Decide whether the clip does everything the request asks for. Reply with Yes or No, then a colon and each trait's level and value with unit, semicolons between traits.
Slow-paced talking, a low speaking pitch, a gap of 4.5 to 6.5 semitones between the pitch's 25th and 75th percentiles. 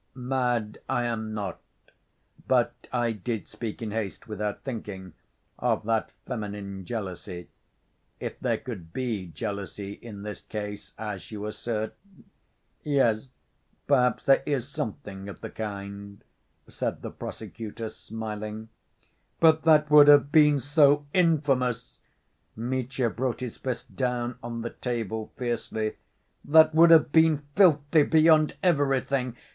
Yes: slow, 125 wpm; low, 120 Hz; average, 4.8 semitones